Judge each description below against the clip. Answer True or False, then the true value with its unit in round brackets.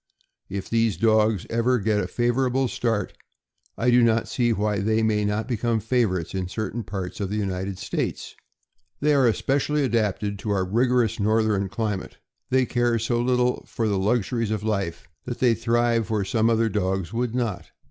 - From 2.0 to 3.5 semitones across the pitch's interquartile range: True (2.8 semitones)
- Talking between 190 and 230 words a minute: False (180 wpm)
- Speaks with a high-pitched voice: False (110 Hz)